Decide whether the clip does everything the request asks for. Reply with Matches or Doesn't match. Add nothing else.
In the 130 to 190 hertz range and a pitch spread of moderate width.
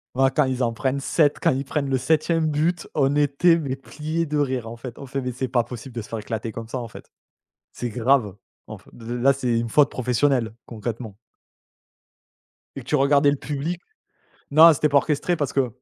Matches